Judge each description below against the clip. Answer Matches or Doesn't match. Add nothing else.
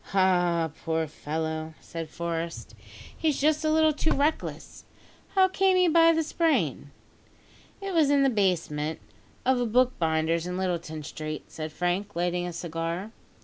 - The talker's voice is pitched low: Doesn't match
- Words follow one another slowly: Doesn't match